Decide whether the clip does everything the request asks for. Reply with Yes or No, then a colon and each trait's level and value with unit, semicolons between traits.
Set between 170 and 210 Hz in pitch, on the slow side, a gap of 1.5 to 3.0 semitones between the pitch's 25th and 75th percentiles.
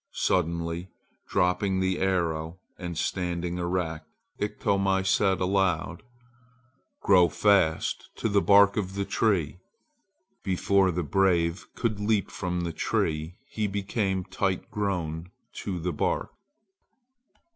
No: very low, 95 Hz; slow, 115 wpm; narrow, 2.5 semitones